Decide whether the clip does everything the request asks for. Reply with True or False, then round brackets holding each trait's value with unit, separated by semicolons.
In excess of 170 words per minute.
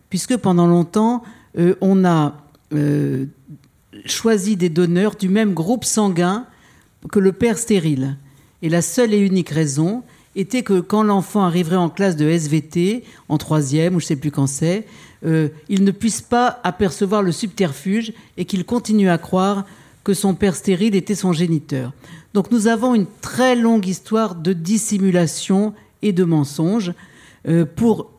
False (160 wpm)